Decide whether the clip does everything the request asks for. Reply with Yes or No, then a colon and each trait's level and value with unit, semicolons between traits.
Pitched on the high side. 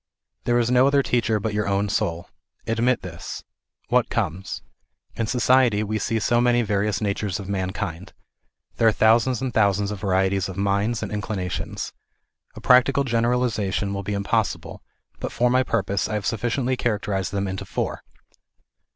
No: low, 105 Hz